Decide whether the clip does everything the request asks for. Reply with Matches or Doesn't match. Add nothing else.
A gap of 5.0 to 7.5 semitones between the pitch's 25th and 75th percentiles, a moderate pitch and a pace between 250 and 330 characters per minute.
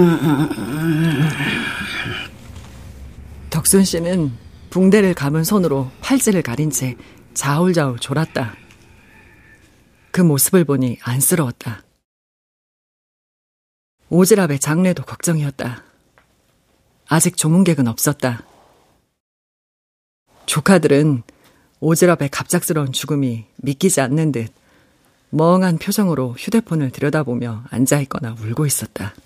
Doesn't match